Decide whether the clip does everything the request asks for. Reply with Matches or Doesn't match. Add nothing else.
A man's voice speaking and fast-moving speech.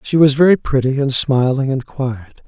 Doesn't match